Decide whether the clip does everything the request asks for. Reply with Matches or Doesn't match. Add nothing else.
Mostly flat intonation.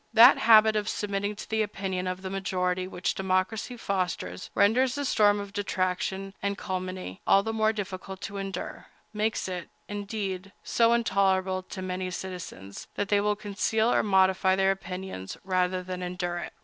Matches